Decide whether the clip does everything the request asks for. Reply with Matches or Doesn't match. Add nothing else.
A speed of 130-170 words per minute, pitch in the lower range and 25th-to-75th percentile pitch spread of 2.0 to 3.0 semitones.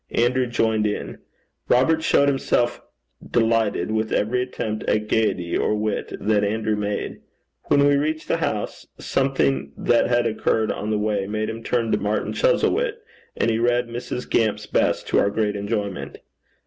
Matches